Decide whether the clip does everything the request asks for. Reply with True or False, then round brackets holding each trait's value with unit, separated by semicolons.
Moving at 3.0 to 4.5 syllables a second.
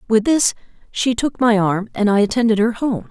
False (5.2 syllables/s)